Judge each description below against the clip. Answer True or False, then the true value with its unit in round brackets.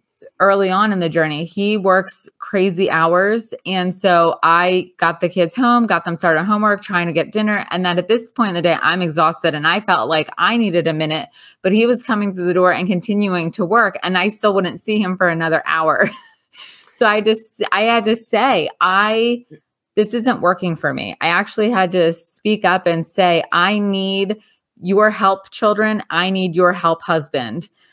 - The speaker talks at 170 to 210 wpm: True (200 wpm)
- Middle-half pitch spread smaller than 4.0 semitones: True (3.6 semitones)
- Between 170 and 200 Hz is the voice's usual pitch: True (190 Hz)